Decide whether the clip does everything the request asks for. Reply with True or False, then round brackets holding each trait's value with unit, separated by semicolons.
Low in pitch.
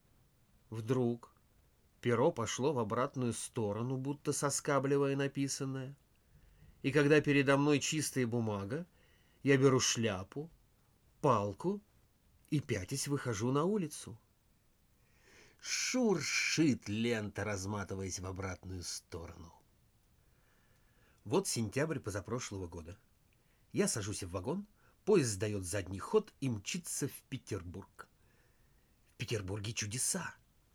True (120 Hz)